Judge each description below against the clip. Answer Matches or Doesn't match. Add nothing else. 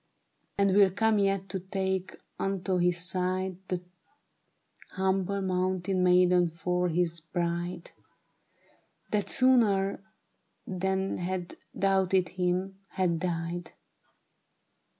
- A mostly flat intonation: Matches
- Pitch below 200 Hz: Matches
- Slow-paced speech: Matches